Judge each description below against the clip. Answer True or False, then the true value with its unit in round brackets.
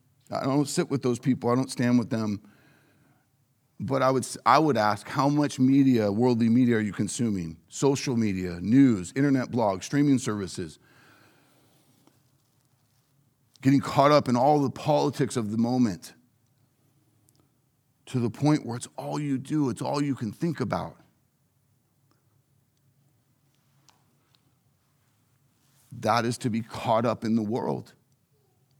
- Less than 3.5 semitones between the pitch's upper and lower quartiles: True (2.6 semitones)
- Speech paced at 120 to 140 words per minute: True (135 wpm)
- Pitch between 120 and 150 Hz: True (130 Hz)